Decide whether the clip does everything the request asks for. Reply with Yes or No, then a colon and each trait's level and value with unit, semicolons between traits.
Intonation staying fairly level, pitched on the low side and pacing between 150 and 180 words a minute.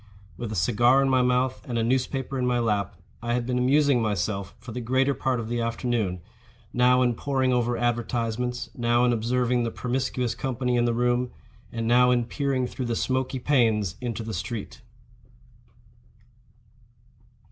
Yes: narrow, 1.6 semitones; low, 120 Hz; average, 170 wpm